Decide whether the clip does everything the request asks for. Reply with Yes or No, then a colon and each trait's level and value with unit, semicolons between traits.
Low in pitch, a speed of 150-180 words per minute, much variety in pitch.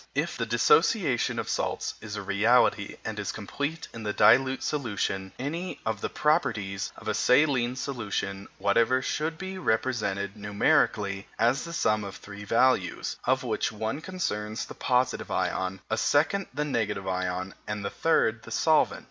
Yes: low, 110 Hz; average, 160 wpm; wide, 5.9 semitones